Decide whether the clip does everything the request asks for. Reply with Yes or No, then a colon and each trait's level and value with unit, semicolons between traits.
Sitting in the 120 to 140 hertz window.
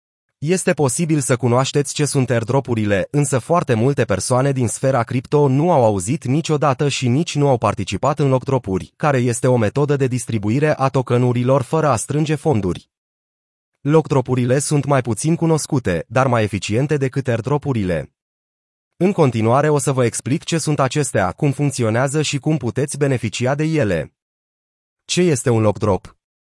Yes: low, 135 Hz